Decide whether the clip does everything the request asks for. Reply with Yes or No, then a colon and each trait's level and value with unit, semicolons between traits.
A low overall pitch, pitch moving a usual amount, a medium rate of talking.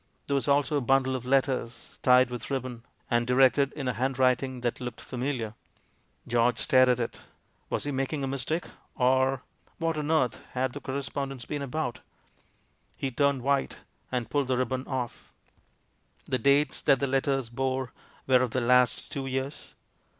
No: low, 130 Hz; narrow, 1.7 semitones; average, 170 wpm